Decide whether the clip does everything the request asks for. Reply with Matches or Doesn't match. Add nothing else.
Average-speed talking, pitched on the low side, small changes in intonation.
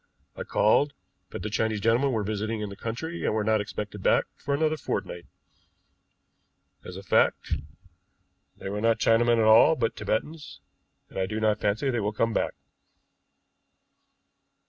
Matches